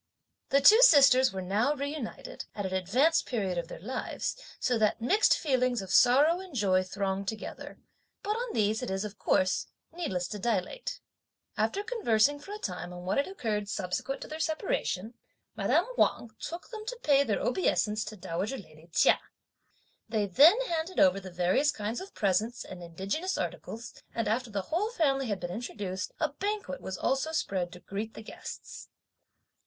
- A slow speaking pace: No, average, 175 wpm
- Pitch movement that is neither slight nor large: No, wide, 7.9 semitones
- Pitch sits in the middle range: No, high, 225 Hz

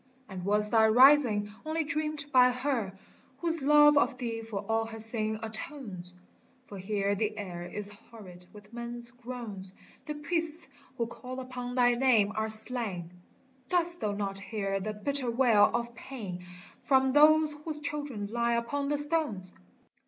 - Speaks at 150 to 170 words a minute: Yes, average, 155 wpm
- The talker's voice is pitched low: No, high, 235 Hz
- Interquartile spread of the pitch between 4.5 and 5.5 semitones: Yes, average, 5.2 semitones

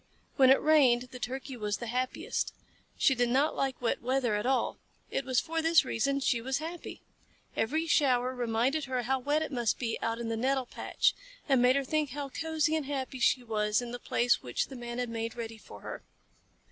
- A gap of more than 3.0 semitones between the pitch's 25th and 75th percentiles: No, narrow, 2.6 semitones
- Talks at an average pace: No, fast, 210 wpm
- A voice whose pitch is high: Yes, very high, 255 Hz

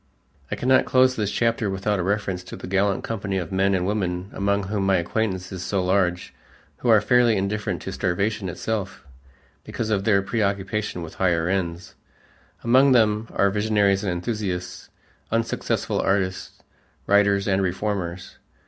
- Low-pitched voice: Yes, low, 100 Hz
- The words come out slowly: No, average, 155 wpm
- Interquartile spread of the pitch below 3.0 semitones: Yes, narrow, 2.4 semitones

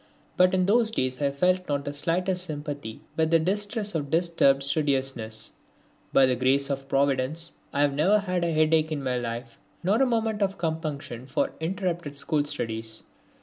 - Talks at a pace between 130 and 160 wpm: No, average, 175 wpm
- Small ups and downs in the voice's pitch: No, average, 4.9 semitones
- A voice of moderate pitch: Yes, medium, 155 Hz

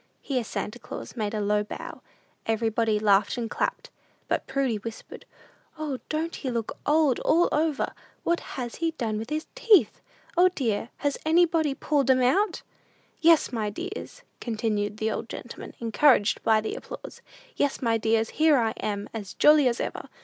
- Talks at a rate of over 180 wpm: No, average, 165 wpm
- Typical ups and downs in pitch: No, wide, 5.8 semitones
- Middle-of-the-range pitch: No, high, 245 Hz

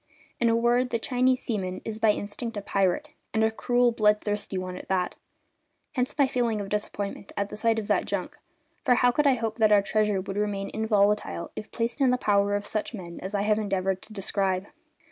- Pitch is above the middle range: Yes, high, 210 Hz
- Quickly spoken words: Yes, fast, 215 wpm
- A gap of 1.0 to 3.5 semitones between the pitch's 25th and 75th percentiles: Yes, average, 2.7 semitones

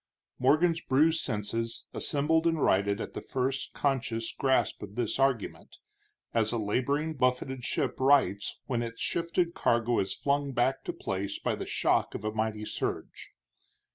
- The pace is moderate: Yes, average, 155 wpm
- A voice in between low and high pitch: No, low, 125 Hz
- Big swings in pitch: No, average, 4.2 semitones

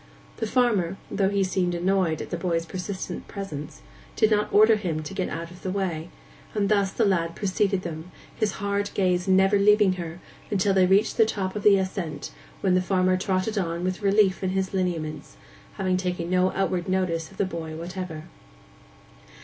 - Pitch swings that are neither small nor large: No, narrow, 2.2 semitones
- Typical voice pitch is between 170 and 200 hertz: Yes, medium, 185 Hz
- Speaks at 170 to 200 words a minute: Yes, average, 180 wpm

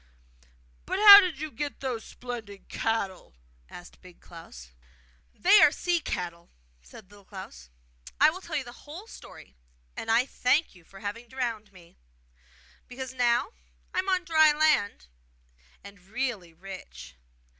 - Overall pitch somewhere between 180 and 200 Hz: No, high, 235 Hz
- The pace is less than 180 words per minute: Yes, average, 145 wpm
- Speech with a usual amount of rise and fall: No, wide, 8.1 semitones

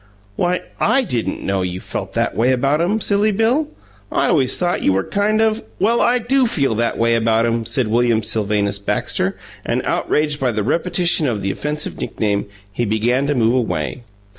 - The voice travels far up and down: Yes, wide, 8.4 semitones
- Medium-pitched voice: No, low, 125 Hz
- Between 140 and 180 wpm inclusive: No, average, 190 wpm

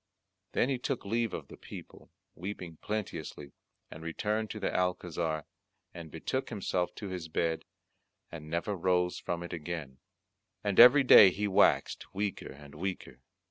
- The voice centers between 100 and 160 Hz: No, very low, 90 Hz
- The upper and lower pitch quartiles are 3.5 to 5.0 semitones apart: Yes, average, 4.1 semitones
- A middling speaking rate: Yes, average, 150 wpm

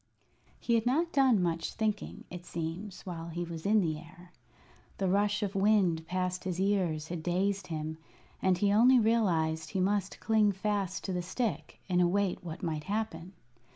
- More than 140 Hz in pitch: Yes, medium, 185 Hz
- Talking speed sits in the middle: Yes, average, 175 wpm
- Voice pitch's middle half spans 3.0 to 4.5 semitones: Yes, average, 3.5 semitones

